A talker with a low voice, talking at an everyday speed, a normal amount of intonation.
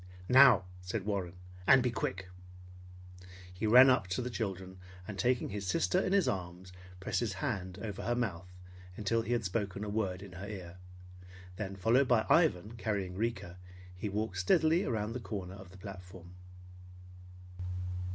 Yes: low, 100 Hz; average, 160 wpm; average, 3.8 semitones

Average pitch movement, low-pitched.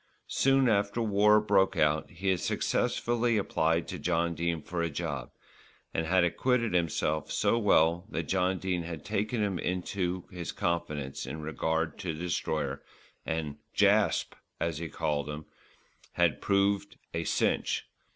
Yes: average, 3.8 semitones; very low, 85 Hz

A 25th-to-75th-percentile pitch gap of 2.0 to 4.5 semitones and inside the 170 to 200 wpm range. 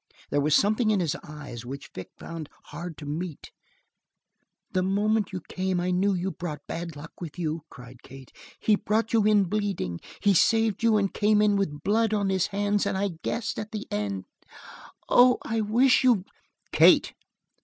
No: wide, 5.6 semitones; average, 185 wpm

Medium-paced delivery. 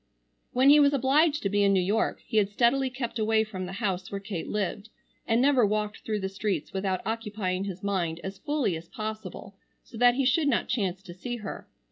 No: fast, 215 wpm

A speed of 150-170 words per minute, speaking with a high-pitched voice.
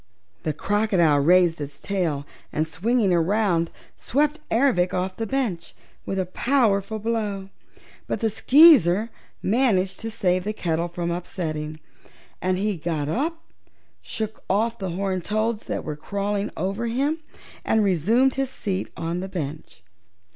No: average, 140 wpm; high, 195 Hz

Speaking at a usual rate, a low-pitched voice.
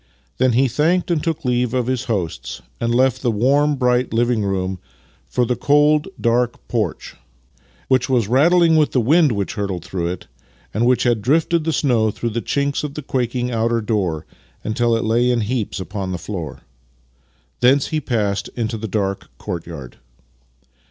Yes: average, 170 wpm; low, 120 Hz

